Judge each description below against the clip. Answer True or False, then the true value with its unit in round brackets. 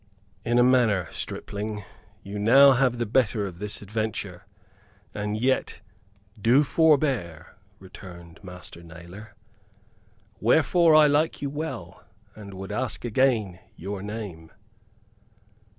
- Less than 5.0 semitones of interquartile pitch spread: False (5.4 semitones)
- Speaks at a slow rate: True (115 wpm)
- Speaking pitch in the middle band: False (105 Hz)